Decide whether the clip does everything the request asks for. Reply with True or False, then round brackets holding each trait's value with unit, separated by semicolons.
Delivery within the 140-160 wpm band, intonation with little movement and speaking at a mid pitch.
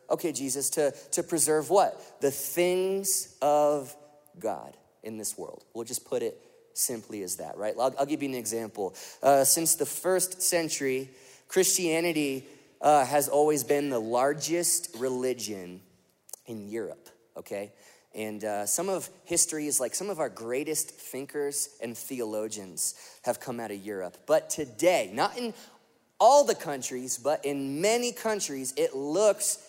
False (150 wpm; 5.3 semitones; 145 Hz)